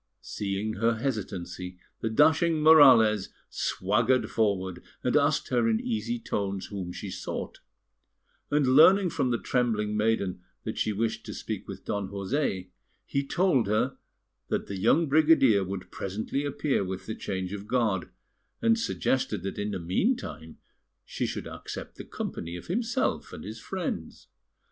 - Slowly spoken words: No, average, 155 wpm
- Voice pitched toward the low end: Yes, low, 110 Hz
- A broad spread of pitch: Yes, wide, 6.0 semitones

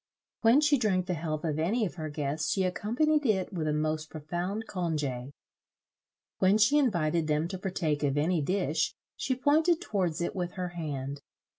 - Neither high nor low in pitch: Yes, medium, 175 Hz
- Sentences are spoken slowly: No, average, 175 wpm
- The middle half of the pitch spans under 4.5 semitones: No, average, 5.2 semitones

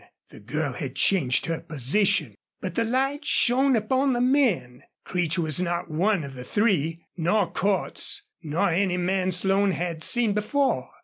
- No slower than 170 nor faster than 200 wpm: No, average, 160 wpm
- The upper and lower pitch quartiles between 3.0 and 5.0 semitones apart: No, wide, 5.4 semitones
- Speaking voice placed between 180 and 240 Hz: Yes, medium, 185 Hz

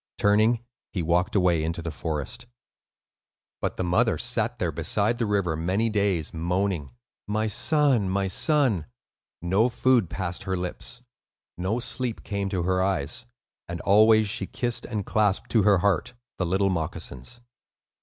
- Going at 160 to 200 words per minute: No, average, 150 wpm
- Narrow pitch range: No, average, 3.8 semitones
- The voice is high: No, low, 100 Hz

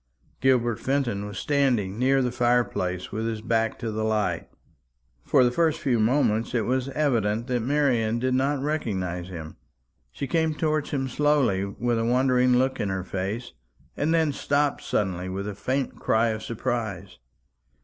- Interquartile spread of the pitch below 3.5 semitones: No, average, 4.2 semitones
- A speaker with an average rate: Yes, average, 170 wpm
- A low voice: Yes, low, 120 Hz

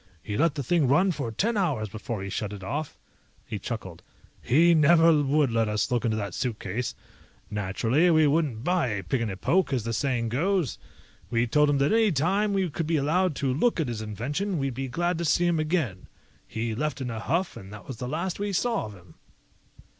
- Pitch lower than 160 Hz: Yes, medium, 140 Hz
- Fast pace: Yes, fast, 220 wpm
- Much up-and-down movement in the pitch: Yes, wide, 6.9 semitones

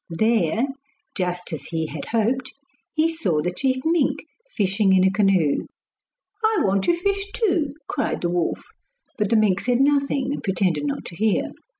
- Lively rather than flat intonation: Yes, wide, 7.7 semitones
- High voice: Yes, high, 215 Hz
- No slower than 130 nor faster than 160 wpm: No, average, 170 wpm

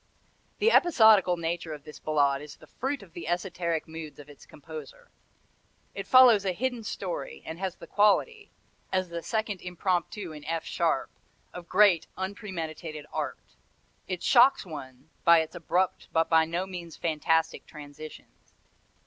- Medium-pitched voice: Yes, medium, 175 Hz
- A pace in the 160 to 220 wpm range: No, average, 150 wpm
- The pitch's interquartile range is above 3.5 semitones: Yes, average, 4.2 semitones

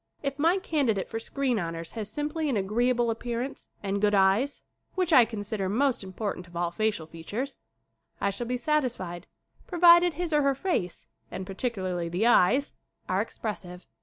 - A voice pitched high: Yes, high, 225 Hz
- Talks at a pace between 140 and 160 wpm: No, average, 170 wpm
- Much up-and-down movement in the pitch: Yes, wide, 6.5 semitones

